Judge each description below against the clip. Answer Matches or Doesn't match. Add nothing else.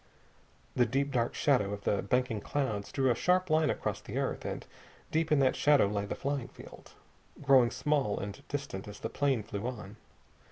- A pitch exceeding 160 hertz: Doesn't match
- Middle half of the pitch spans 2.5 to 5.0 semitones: Doesn't match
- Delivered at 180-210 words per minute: Matches